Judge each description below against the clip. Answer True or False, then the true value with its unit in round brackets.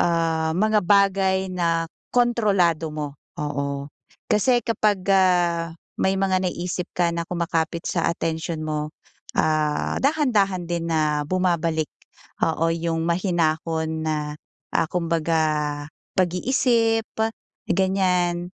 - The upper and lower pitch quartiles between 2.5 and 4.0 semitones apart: True (2.8 semitones)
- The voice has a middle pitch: True (170 Hz)